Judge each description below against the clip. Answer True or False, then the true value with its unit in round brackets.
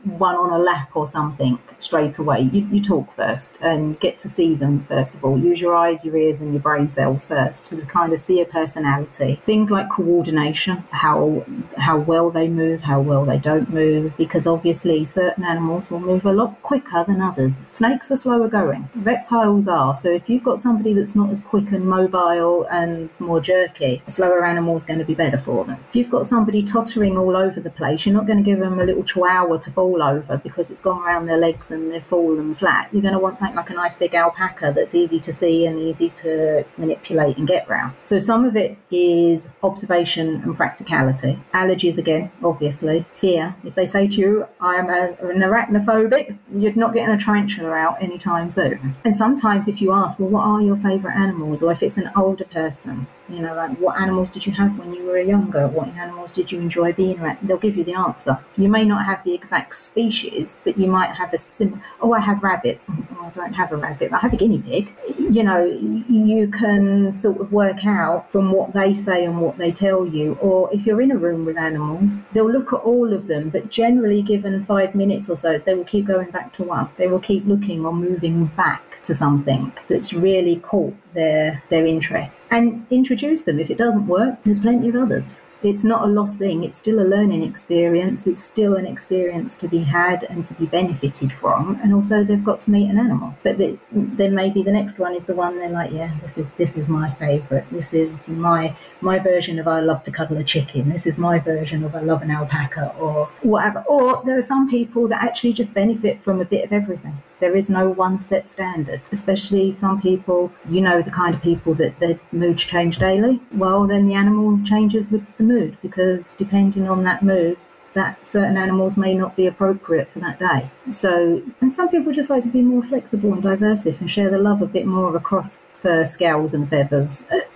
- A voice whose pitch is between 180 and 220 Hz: True (185 Hz)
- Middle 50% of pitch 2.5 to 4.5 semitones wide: True (3.7 semitones)